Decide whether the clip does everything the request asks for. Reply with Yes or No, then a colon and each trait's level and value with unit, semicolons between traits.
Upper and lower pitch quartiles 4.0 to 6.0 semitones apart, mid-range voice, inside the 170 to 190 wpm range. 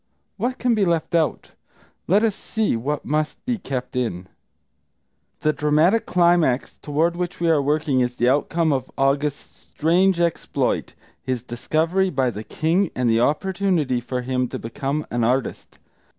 No: wide, 5.4 semitones; medium, 150 Hz; average, 155 wpm